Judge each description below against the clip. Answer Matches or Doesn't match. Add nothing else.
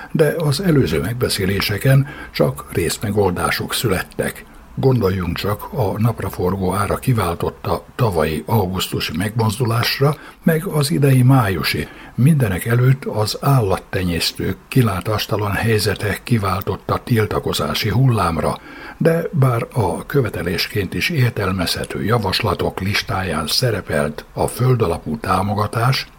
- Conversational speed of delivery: Doesn't match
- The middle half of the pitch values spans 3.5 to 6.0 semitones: Matches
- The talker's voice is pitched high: Doesn't match